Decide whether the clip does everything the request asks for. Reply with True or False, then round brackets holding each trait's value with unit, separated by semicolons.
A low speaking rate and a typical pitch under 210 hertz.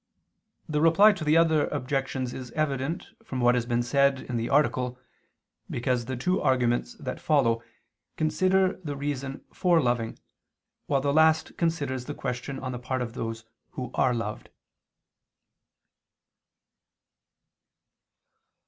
True (130 wpm; 135 Hz)